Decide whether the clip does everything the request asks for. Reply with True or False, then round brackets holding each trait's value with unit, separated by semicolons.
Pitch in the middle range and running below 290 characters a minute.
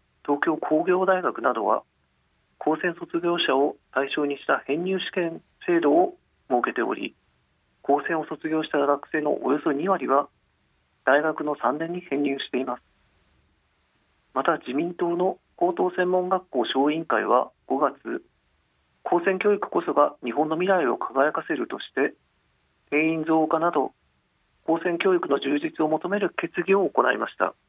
True (160 Hz; 265 characters per minute)